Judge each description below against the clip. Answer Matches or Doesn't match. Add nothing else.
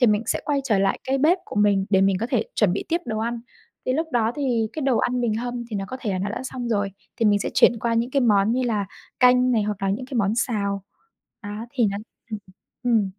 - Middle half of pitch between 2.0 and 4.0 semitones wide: Matches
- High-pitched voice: Matches